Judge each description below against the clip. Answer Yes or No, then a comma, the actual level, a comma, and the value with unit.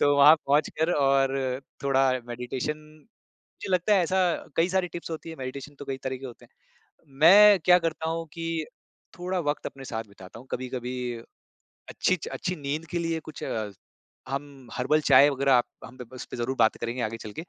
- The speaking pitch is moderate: Yes, medium, 145 Hz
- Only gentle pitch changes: No, average, 4.2 semitones